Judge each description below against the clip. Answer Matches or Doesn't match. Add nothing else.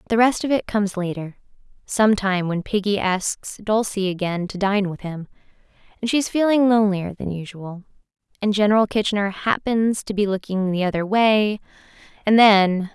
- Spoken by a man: Doesn't match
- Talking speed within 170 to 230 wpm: Doesn't match